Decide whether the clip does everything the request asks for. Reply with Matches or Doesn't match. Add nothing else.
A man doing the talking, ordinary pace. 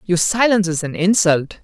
Matches